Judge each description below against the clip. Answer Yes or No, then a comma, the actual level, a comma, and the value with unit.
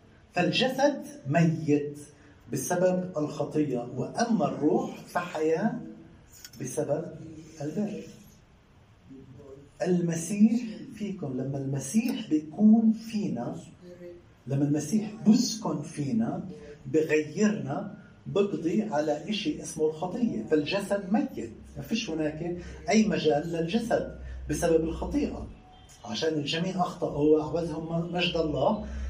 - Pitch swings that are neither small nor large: No, wide, 5.9 semitones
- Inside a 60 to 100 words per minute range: Yes, average, 85 wpm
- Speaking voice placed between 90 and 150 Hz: No, medium, 160 Hz